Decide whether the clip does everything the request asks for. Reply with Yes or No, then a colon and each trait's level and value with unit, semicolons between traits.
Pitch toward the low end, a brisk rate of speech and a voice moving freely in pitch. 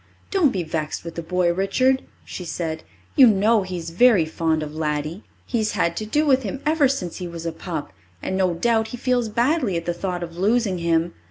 No: medium, 185 Hz; fast, 220 wpm; wide, 5.8 semitones